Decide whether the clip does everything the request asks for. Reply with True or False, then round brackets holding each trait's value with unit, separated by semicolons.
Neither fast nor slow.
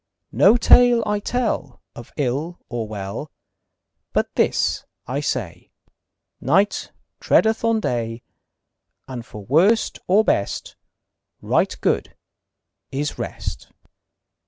False (105 wpm)